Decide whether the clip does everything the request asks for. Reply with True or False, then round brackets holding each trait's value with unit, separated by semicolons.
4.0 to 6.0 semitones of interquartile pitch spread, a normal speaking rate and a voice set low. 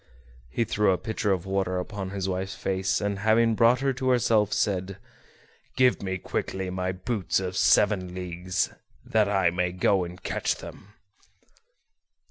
False (2.5 semitones; 155 wpm; 95 Hz)